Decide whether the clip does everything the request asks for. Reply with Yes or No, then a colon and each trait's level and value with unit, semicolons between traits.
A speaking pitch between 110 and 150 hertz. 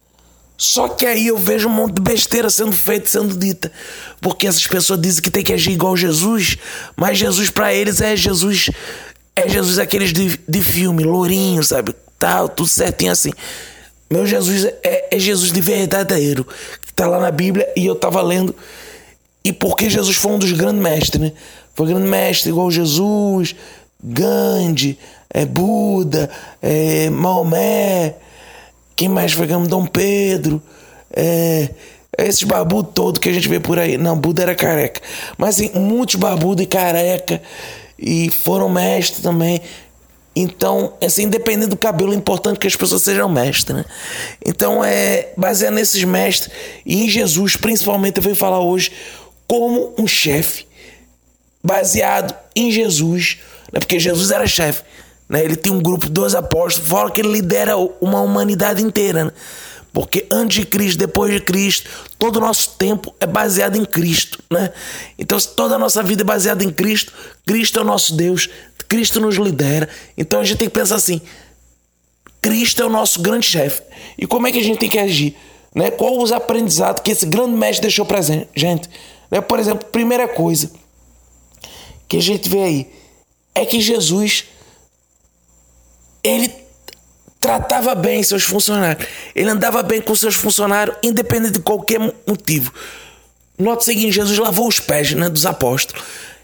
No: high, 190 Hz